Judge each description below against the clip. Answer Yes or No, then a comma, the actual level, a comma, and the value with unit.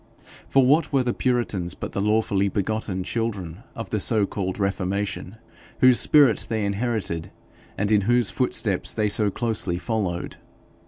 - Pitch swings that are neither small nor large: Yes, average, 3.3 semitones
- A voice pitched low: Yes, low, 105 Hz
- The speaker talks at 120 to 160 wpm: Yes, average, 150 wpm